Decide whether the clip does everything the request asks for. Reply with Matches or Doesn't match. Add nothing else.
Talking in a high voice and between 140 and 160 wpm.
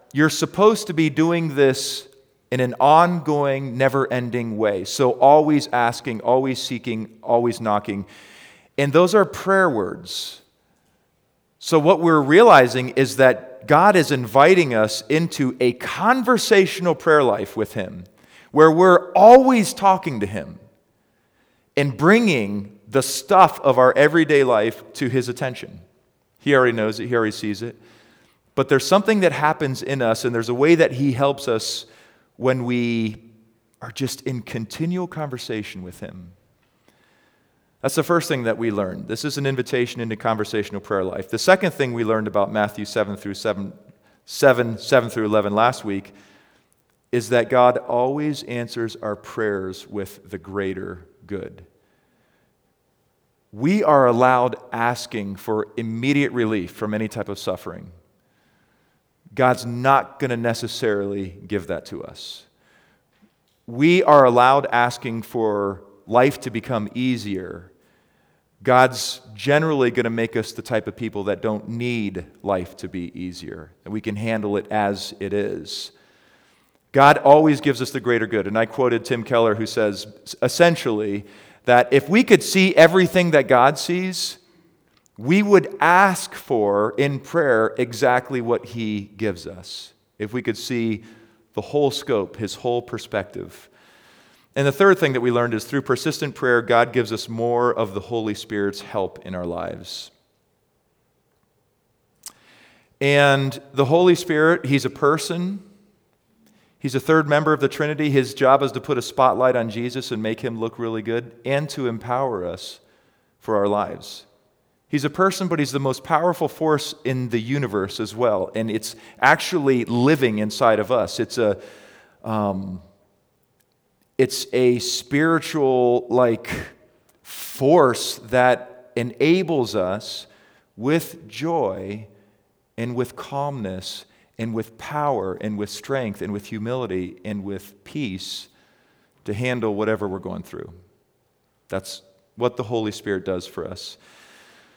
Doesn't match